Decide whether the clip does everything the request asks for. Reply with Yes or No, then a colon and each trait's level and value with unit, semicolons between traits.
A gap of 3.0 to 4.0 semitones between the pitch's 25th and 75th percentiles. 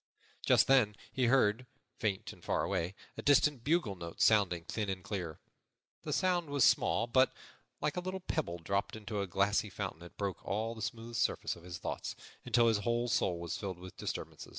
No: average, 4.7 semitones